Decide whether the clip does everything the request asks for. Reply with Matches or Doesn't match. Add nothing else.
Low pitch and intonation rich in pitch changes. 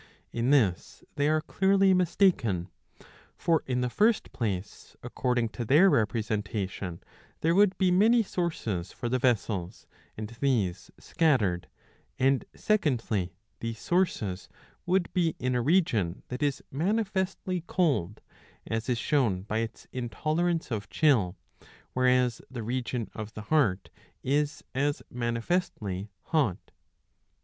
Matches